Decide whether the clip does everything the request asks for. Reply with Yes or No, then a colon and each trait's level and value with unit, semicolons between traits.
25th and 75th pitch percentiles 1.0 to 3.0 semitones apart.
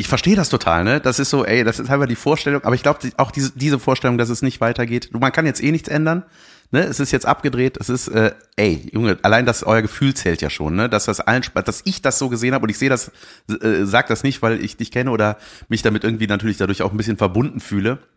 No: average, 3.8 semitones